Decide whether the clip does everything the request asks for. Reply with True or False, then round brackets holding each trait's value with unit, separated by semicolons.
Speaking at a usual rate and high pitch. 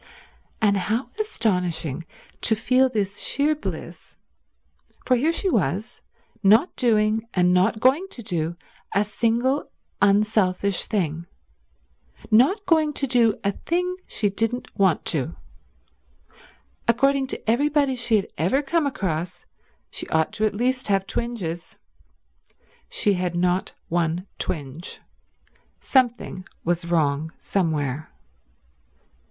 False (120 wpm; 210 Hz)